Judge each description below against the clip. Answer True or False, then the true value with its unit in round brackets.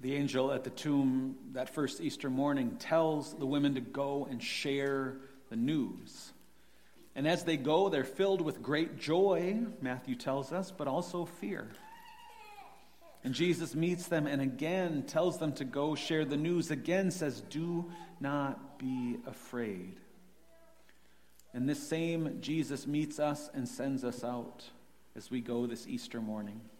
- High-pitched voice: False (140 Hz)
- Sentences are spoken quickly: False (150 wpm)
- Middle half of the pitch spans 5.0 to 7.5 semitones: False (4.2 semitones)